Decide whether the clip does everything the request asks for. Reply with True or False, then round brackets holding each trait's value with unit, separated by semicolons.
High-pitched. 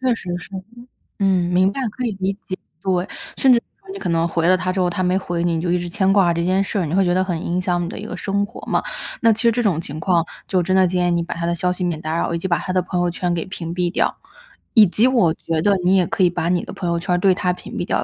False (180 Hz)